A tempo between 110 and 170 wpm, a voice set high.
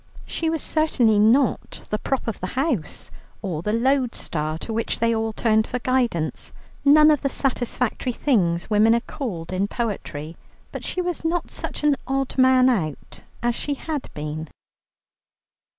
Yes: average, 160 wpm; high, 235 Hz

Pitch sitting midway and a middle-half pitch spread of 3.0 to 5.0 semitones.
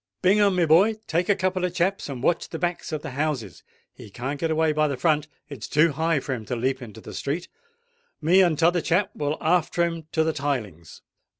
Yes: medium, 155 Hz; average, 3.9 semitones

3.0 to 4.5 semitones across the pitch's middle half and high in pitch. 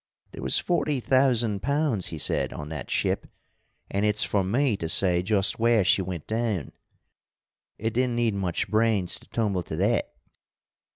No: average, 4.1 semitones; low, 105 Hz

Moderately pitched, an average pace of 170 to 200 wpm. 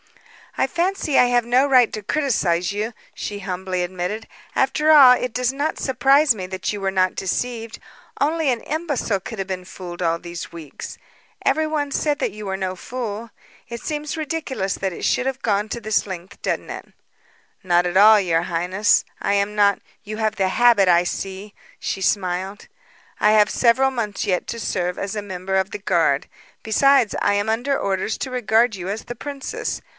No: high, 210 Hz; average, 190 wpm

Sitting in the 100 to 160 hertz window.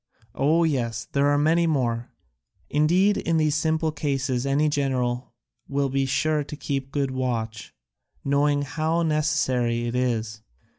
Yes: medium, 140 Hz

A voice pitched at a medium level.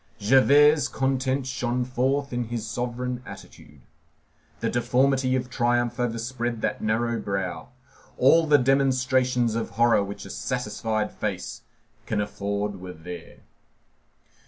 No: low, 120 Hz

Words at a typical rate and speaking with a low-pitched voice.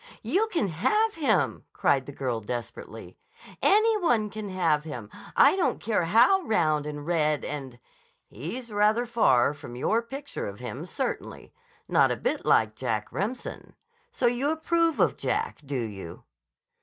No: average, 155 wpm; high, 190 Hz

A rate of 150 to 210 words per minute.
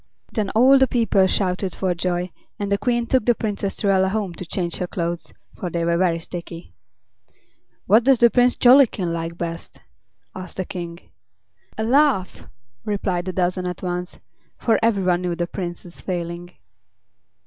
Yes: average, 165 wpm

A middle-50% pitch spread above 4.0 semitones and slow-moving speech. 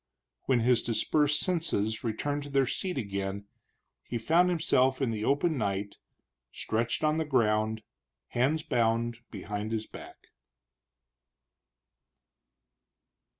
Yes: average, 5.1 semitones; slow, 110 wpm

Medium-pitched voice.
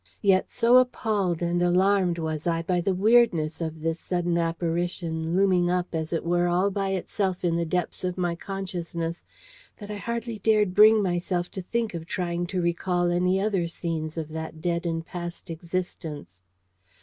Yes: medium, 175 Hz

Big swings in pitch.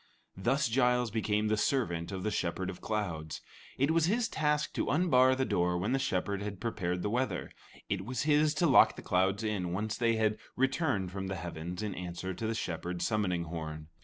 Yes: wide, 6.0 semitones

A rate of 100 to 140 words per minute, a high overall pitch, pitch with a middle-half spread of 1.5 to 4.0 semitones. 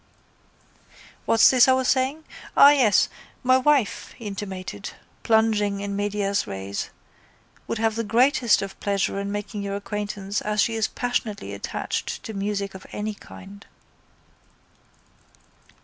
Yes: slow, 135 wpm; high, 210 Hz; narrow, 2.4 semitones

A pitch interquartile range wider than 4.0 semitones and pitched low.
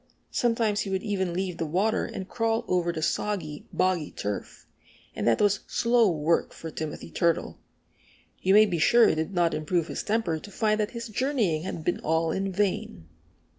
No: average, 4.5 semitones; medium, 185 Hz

